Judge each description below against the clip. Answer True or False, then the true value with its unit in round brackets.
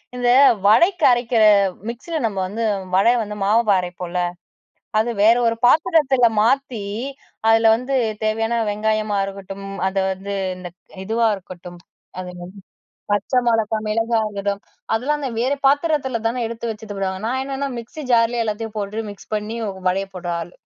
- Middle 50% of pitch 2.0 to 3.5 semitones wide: True (3.2 semitones)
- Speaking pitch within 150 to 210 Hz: False (225 Hz)